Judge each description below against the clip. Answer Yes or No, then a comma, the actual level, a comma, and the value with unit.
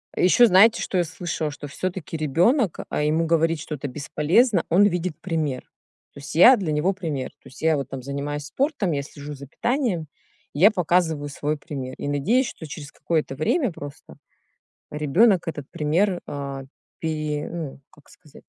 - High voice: No, medium, 160 Hz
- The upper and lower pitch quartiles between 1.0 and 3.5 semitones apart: No, average, 4.0 semitones